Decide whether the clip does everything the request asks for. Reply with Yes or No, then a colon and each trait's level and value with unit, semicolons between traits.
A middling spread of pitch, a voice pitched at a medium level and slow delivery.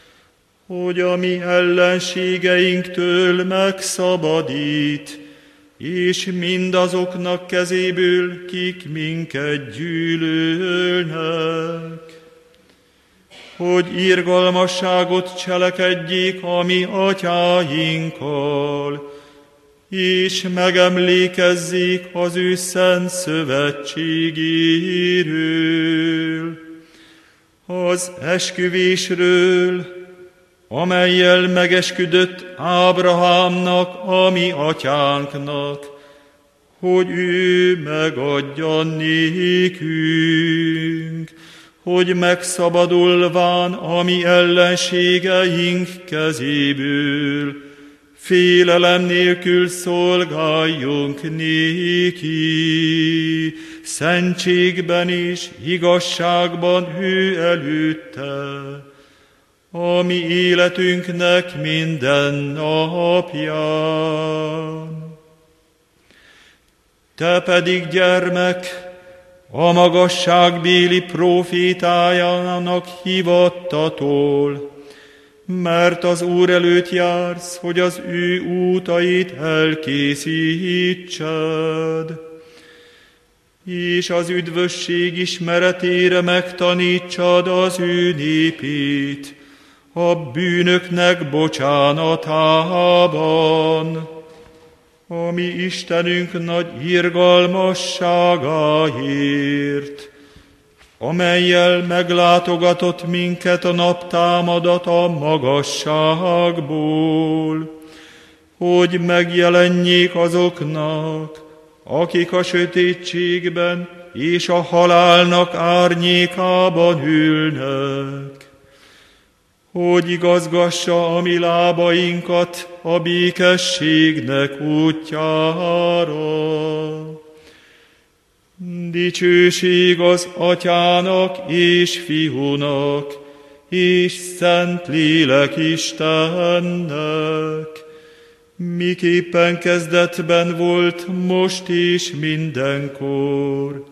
No: narrow, 2.2 semitones; medium, 175 Hz; slow, 55 wpm